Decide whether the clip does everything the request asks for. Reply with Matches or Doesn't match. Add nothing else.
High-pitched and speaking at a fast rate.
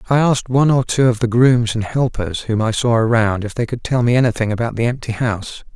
Doesn't match